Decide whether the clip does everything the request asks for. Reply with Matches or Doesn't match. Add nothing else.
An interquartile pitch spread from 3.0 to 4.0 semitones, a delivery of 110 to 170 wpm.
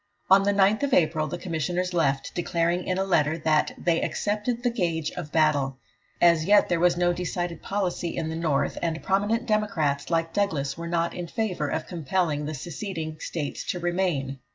Doesn't match